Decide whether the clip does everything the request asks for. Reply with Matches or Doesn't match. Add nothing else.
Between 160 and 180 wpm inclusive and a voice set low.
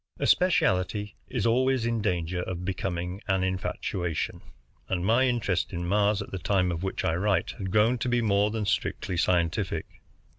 Matches